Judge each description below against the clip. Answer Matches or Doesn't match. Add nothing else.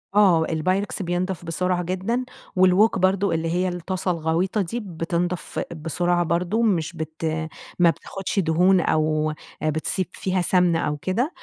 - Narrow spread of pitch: Matches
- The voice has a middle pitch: Matches